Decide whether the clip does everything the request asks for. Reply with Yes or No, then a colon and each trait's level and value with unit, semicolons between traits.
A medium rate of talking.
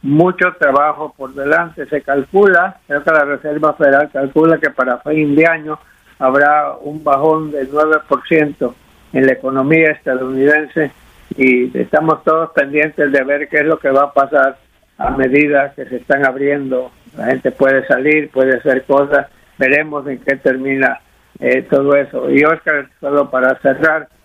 Yes: average, 160 wpm